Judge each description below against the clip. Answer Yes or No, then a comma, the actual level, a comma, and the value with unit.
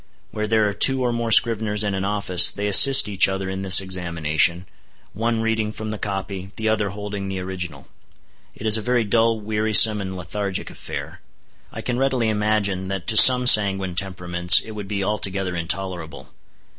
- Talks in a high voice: No, low, 100 Hz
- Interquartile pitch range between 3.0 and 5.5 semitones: No, narrow, 2.6 semitones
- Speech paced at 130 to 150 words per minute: No, average, 180 wpm